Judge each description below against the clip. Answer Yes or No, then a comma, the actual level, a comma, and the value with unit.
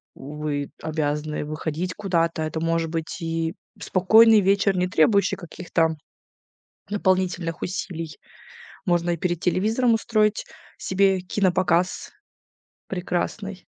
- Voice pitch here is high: No, medium, 175 Hz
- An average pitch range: Yes, average, 3.1 semitones